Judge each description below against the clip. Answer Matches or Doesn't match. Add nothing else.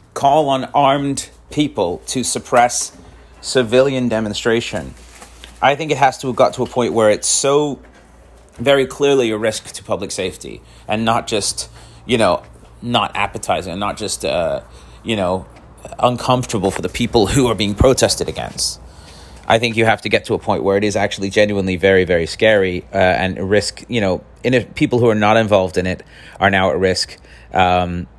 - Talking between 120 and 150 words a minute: Doesn't match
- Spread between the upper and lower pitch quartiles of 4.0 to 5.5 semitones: Matches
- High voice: Doesn't match